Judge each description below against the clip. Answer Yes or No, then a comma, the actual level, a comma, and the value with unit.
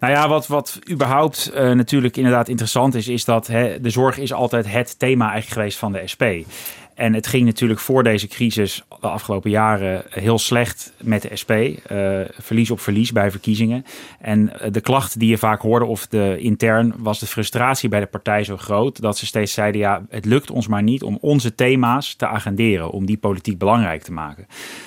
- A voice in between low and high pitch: No, low, 115 Hz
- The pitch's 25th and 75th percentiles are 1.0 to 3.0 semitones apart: Yes, average, 2.7 semitones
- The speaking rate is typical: No, fast, 205 wpm